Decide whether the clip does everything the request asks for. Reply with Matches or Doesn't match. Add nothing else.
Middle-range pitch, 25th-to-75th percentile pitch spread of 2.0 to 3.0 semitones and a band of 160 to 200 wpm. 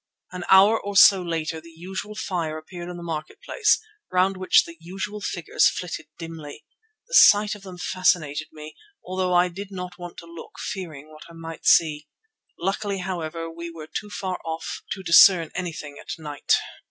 Matches